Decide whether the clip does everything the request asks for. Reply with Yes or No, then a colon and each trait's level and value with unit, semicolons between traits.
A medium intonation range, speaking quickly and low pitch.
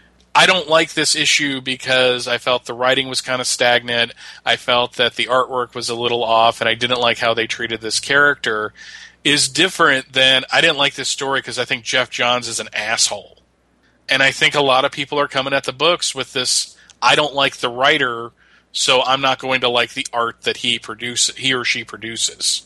No: narrow, 2.3 semitones; fast, 220 wpm; low, 125 Hz